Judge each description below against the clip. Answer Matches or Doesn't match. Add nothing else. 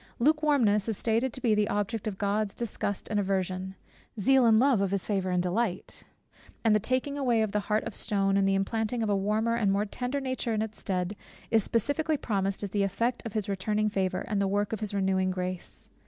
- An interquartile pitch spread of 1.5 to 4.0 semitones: Matches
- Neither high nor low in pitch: Doesn't match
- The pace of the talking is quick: Matches